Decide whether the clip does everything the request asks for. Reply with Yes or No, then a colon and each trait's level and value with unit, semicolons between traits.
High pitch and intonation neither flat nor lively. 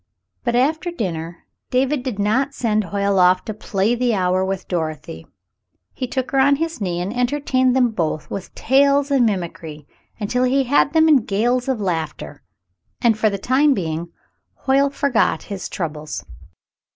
No: high, 225 Hz; wide, 6.4 semitones